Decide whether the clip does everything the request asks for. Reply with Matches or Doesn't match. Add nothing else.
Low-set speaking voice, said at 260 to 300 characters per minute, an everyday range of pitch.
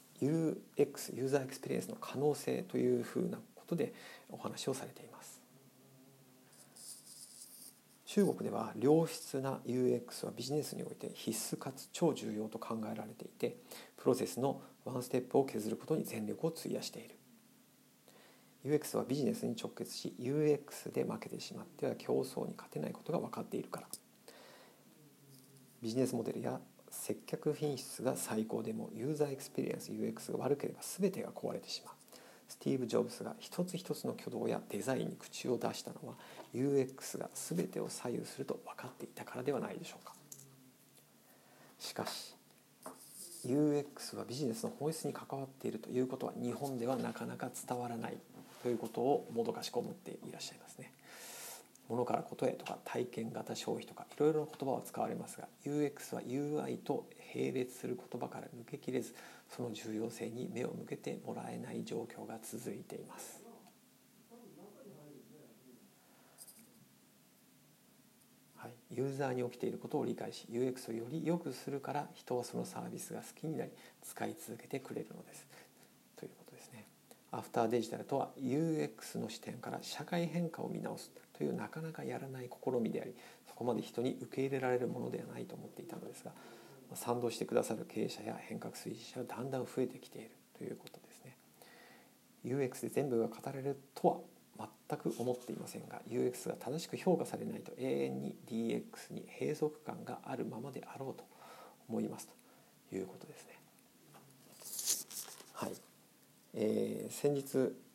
Doesn't match